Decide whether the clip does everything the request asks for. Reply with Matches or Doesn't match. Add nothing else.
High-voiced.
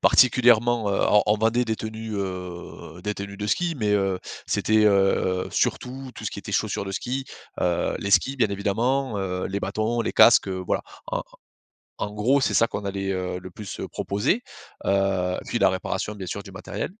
Doesn't match